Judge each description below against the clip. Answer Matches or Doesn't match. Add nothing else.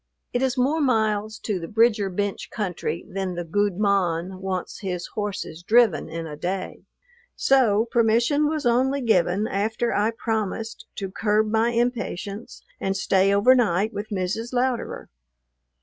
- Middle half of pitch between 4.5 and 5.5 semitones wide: Doesn't match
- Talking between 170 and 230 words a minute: Doesn't match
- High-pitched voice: Matches